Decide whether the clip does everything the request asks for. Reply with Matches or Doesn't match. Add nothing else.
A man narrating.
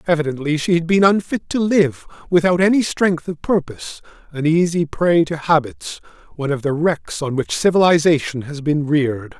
Matches